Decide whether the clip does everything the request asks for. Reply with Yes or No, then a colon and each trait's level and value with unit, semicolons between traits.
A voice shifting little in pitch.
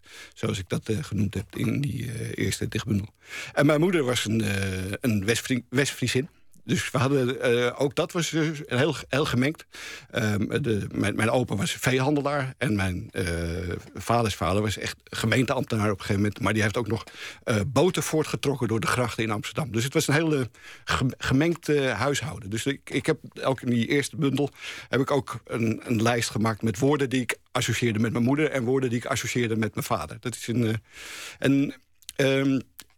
No: average, 3.9 semitones